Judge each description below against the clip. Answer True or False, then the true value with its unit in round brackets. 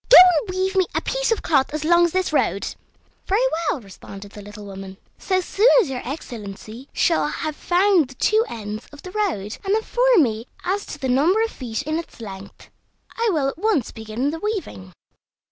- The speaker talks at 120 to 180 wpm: False (200 wpm)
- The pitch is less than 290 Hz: False (300 Hz)